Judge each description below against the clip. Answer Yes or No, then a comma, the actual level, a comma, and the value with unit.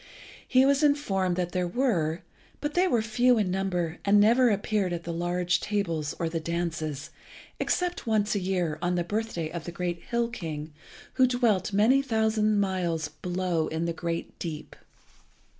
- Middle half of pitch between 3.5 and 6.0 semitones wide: Yes, average, 4.6 semitones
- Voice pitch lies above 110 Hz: Yes, medium, 185 Hz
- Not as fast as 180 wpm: Yes, average, 170 wpm